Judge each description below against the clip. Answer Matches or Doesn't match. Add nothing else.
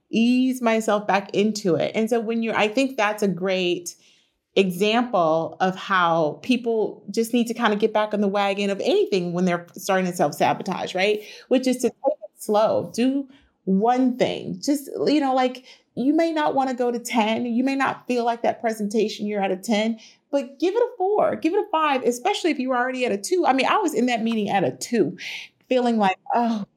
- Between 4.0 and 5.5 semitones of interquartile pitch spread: Matches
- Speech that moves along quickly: Matches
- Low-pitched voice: Doesn't match